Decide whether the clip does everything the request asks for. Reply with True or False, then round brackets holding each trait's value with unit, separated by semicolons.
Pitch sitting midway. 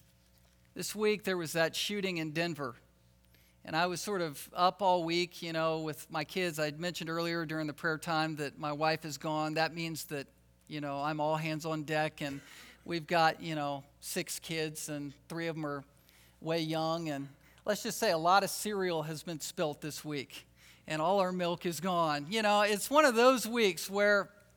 True (160 Hz)